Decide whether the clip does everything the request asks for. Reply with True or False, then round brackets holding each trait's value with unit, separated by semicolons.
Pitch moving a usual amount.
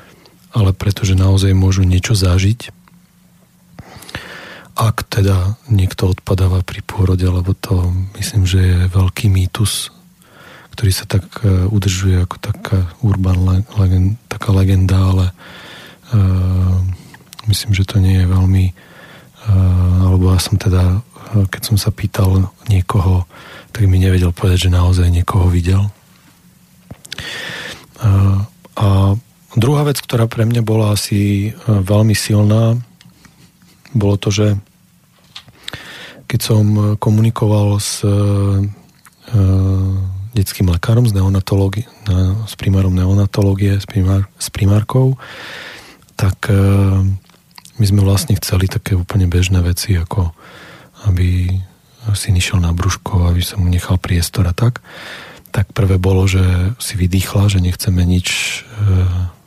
False (2.3 semitones)